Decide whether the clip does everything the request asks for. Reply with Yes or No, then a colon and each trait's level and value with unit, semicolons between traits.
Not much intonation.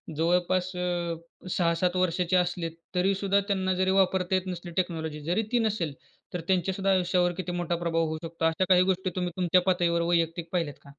Yes: narrow, 1.7 semitones